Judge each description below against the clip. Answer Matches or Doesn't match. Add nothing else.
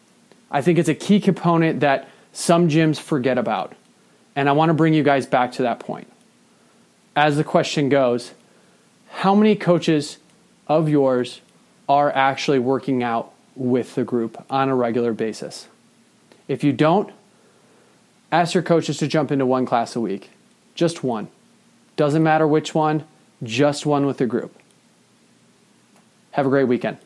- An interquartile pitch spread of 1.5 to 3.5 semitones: Doesn't match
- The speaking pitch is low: Doesn't match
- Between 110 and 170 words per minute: Matches